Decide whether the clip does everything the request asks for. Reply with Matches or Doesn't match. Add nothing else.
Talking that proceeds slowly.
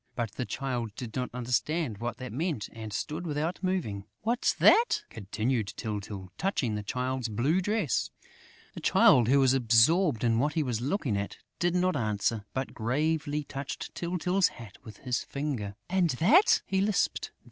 Doesn't match